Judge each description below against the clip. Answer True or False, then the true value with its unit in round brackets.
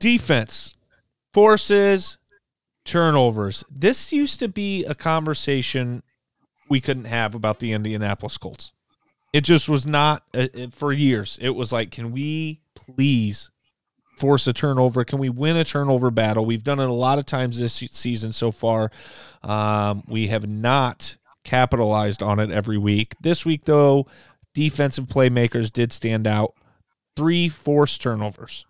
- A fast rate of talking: False (140 wpm)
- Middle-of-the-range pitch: False (130 Hz)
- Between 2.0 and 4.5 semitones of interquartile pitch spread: False (4.9 semitones)